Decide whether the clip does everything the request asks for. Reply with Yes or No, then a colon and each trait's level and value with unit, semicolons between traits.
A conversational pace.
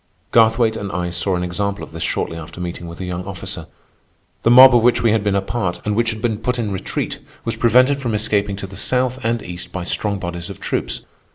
No: fast, 240 wpm